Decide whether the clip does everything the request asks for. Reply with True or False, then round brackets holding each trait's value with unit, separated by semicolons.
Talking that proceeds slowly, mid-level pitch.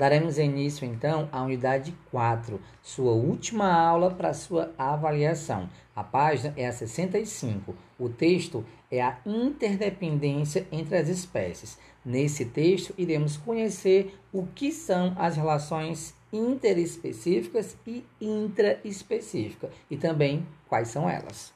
True (115 wpm; 160 Hz)